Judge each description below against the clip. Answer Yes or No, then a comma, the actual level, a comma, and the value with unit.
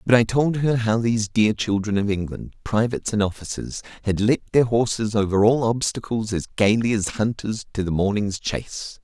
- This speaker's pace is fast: No, average, 185 wpm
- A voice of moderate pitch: No, low, 110 Hz